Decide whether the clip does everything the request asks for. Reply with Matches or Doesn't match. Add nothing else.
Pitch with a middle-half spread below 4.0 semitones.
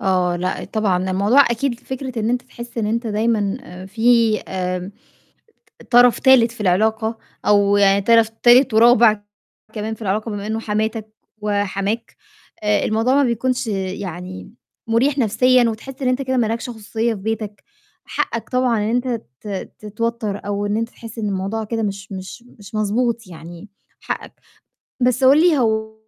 Matches